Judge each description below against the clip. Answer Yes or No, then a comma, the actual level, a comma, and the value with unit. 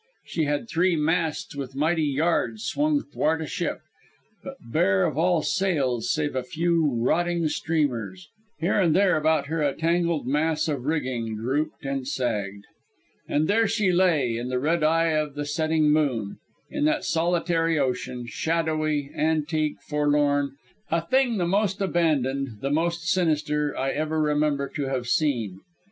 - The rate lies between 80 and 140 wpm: No, average, 155 wpm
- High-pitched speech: No, medium, 150 Hz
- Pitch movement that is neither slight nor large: Yes, average, 3.4 semitones